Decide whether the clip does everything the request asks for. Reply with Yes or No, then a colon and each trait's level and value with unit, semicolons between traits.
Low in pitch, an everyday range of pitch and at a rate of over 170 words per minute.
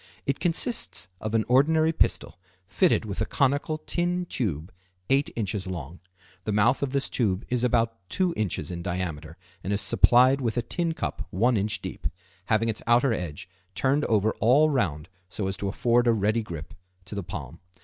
No: low, 115 Hz; wide, 6.0 semitones; average, 180 wpm